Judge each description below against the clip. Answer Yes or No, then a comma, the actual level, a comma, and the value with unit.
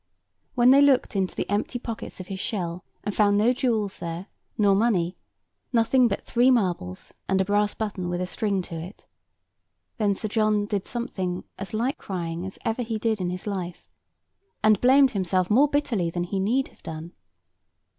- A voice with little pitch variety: No, average, 4.0 semitones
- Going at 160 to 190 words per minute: Yes, average, 175 wpm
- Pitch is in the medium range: No, high, 205 Hz